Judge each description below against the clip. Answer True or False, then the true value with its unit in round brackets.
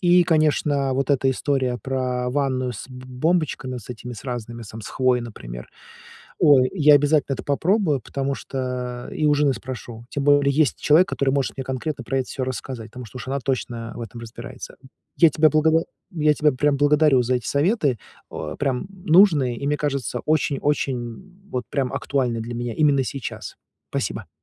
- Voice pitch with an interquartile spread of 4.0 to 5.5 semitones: False (3.0 semitones)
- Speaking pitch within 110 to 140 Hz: True (135 Hz)